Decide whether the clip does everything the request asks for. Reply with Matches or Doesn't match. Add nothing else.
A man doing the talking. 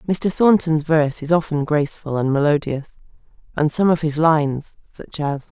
Doesn't match